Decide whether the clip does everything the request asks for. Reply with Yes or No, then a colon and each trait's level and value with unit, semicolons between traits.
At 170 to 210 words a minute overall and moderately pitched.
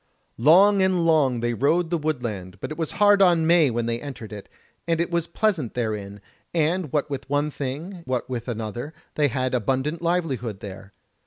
Yes: average, 185 wpm; medium, 145 Hz